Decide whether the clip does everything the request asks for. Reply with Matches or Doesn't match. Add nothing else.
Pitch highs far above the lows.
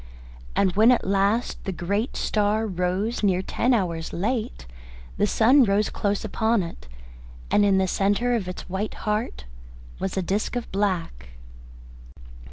Doesn't match